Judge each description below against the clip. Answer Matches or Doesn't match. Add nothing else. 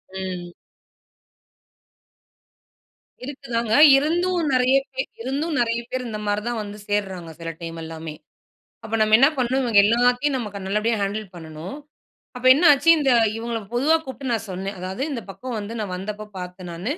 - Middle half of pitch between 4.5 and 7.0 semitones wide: Matches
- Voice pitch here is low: Doesn't match